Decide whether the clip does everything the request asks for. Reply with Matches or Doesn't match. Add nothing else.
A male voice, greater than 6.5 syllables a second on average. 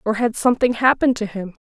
Doesn't match